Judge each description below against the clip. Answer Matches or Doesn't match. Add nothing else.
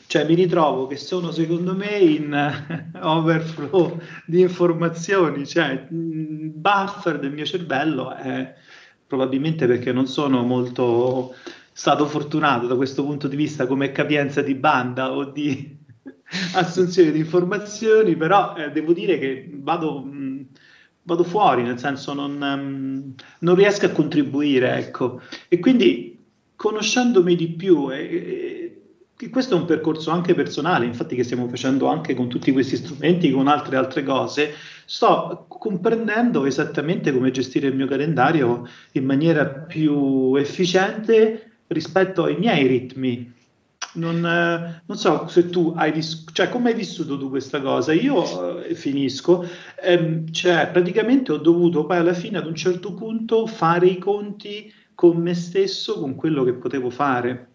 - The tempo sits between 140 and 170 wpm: Matches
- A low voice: Doesn't match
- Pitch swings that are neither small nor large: Matches